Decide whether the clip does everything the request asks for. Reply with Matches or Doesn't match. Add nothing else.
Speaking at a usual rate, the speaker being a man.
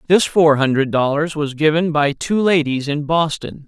Matches